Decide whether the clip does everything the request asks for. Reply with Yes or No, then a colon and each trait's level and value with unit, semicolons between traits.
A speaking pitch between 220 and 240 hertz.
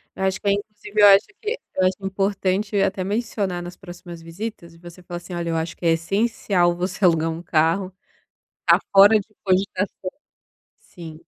No: medium, 185 Hz